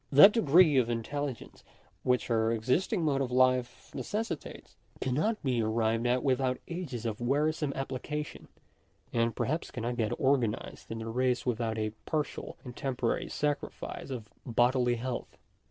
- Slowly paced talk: No, average, 145 wpm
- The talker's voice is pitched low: Yes, low, 125 Hz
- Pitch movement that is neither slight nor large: Yes, average, 3.6 semitones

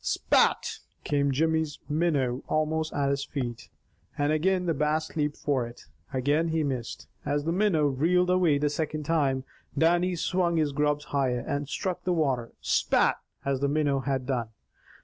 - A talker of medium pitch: Yes, medium, 150 Hz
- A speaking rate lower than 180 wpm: Yes, average, 165 wpm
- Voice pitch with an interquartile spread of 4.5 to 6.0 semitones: No, average, 2.8 semitones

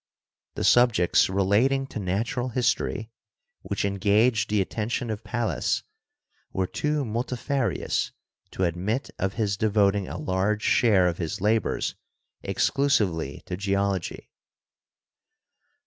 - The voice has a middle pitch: No, low, 105 Hz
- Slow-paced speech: Yes, slow, 110 wpm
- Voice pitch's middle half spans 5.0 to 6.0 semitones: No, average, 3.8 semitones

